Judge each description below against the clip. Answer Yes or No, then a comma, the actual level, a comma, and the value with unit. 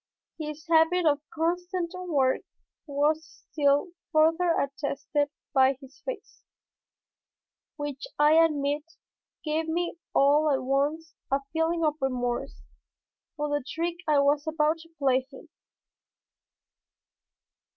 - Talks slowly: Yes, slow, 110 wpm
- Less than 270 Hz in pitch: No, very high, 300 Hz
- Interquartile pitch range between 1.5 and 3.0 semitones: Yes, narrow, 2.5 semitones